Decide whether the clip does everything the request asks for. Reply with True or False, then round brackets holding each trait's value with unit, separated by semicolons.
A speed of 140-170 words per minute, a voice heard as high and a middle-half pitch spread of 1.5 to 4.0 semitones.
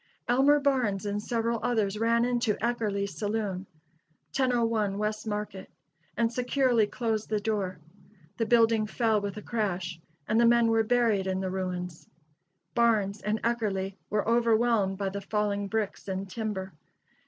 True (145 wpm; 215 Hz; 2.8 semitones)